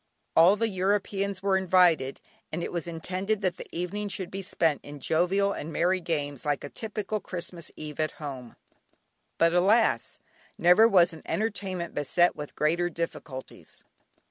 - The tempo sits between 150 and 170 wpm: Yes, average, 155 wpm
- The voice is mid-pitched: Yes, medium, 175 Hz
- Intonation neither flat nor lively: Yes, average, 3.5 semitones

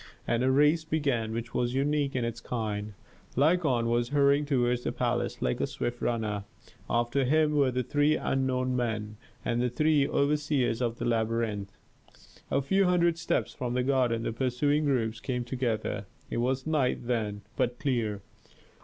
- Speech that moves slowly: No, average, 165 wpm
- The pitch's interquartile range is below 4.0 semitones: Yes, average, 3.4 semitones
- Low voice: Yes, low, 125 Hz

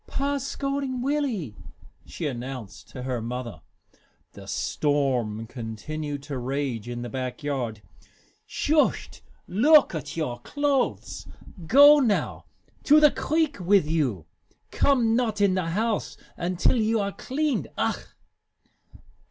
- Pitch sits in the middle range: Yes, medium, 165 Hz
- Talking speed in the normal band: No, slow, 120 wpm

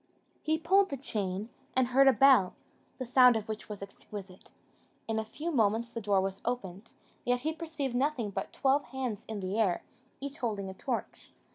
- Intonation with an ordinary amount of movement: Yes, average, 4.9 semitones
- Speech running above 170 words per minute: Yes, average, 185 wpm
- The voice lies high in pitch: Yes, high, 235 Hz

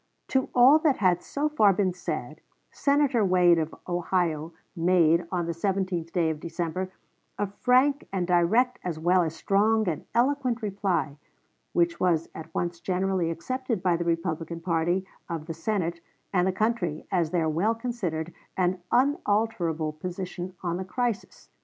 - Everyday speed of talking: Yes, average, 155 wpm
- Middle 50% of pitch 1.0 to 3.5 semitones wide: No, average, 4.3 semitones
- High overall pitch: No, medium, 180 Hz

